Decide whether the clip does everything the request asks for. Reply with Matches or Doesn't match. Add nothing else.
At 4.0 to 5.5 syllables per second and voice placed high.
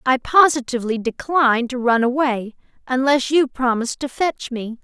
Matches